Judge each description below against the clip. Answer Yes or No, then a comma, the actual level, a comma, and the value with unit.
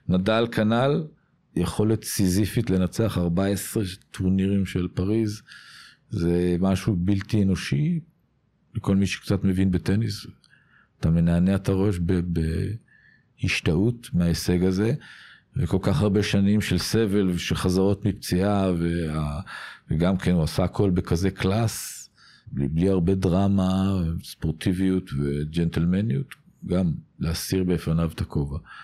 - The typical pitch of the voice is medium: No, very low, 95 Hz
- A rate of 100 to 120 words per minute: Yes, average, 110 wpm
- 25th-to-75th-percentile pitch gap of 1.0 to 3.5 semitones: Yes, average, 3.0 semitones